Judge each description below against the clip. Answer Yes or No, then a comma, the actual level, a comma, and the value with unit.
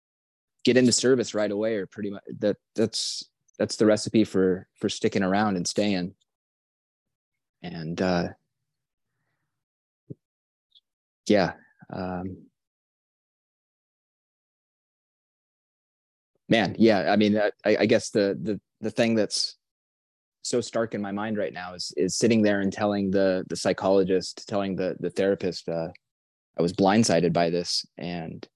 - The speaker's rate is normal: No, slow, 130 wpm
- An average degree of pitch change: Yes, average, 3.2 semitones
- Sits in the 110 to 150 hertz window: No, low, 100 Hz